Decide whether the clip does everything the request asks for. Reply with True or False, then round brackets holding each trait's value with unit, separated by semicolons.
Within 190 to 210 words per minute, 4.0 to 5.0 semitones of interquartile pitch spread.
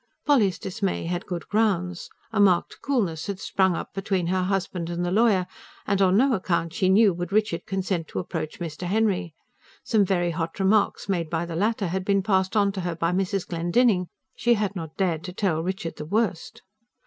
False (195 wpm; 2.8 semitones)